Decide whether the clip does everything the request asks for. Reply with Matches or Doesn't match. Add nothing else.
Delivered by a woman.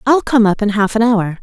Matches